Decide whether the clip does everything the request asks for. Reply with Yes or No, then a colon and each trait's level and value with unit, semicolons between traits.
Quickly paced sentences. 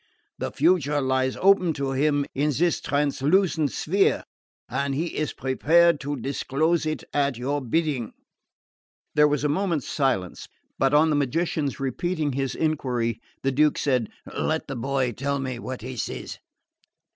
No: average, 150 wpm